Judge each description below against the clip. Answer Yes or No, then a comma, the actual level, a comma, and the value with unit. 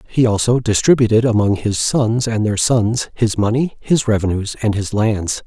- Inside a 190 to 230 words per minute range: No, average, 175 wpm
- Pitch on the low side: Yes, low, 110 Hz